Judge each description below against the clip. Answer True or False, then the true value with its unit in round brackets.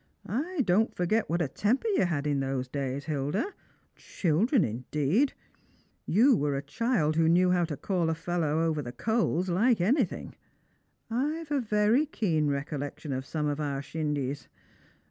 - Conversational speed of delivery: True (160 wpm)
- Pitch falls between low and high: True (165 Hz)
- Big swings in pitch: True (7.3 semitones)